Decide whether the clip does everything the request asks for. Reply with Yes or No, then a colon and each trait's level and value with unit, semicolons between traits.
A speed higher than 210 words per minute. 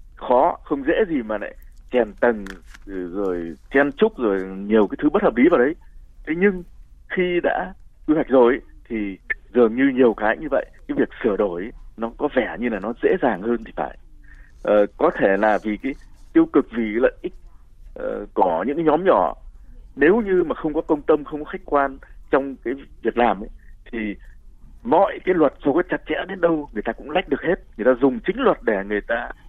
Yes: average, 220 wpm